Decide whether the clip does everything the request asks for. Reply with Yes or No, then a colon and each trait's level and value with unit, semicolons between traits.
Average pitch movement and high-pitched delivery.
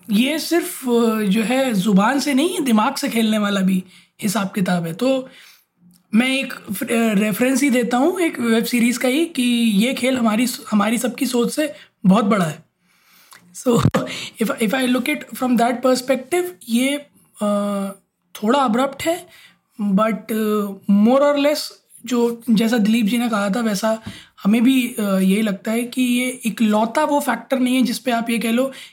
Yes: average, 3.6 semitones; high, 235 Hz